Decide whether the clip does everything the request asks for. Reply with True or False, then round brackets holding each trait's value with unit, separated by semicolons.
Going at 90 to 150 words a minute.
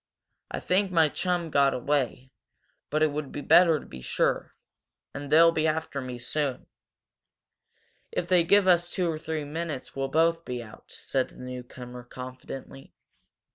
False (160 wpm)